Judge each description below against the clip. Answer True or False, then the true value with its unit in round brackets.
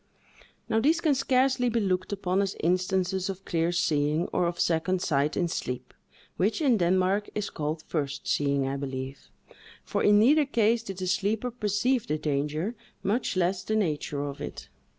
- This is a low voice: False (185 Hz)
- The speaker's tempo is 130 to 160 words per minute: False (170 wpm)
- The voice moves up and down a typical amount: False (5.7 semitones)